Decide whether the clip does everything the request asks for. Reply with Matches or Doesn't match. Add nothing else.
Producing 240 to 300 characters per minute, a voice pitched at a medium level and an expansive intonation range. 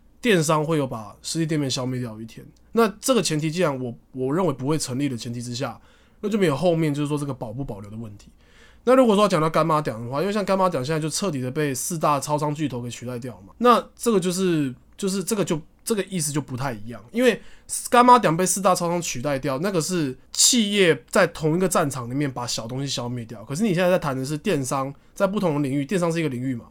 Doesn't match